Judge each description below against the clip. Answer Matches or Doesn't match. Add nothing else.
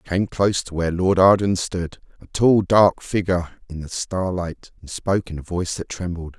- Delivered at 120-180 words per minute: Doesn't match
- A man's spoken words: Matches